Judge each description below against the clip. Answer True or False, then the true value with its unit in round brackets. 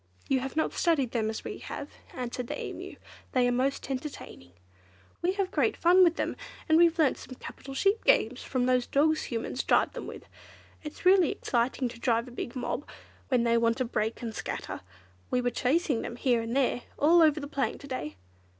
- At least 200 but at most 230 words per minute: True (205 wpm)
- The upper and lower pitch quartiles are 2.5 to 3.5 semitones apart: False (4.6 semitones)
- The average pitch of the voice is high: True (260 Hz)